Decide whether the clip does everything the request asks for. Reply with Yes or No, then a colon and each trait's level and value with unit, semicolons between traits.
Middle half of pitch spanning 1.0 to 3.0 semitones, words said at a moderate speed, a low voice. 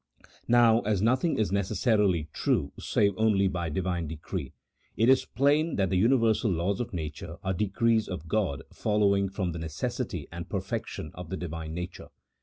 No: average, 4.4 semitones; average, 170 wpm; very low, 95 Hz